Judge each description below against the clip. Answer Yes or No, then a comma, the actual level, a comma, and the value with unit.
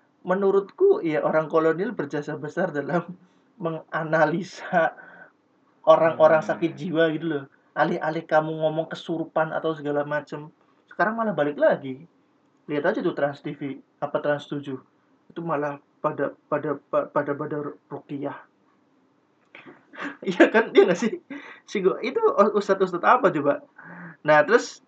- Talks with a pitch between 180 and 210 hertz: No, medium, 160 Hz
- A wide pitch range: No, average, 3.5 semitones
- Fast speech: No, average, 130 wpm